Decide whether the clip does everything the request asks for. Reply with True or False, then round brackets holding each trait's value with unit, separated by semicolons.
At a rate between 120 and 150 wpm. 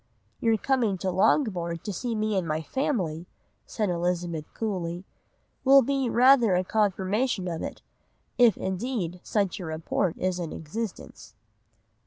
True (140 wpm)